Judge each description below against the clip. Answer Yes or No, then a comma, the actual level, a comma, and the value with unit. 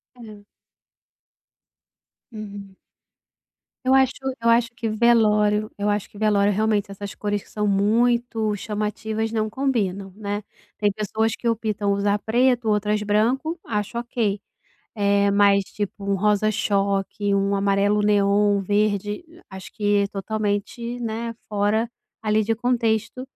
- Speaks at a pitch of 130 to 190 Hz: No, high, 210 Hz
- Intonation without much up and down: Yes, narrow, 1.8 semitones